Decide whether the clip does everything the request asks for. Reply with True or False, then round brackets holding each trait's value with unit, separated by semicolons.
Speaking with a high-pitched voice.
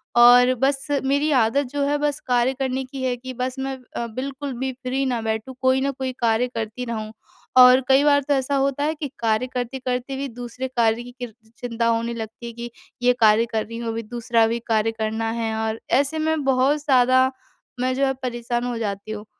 True (250 Hz)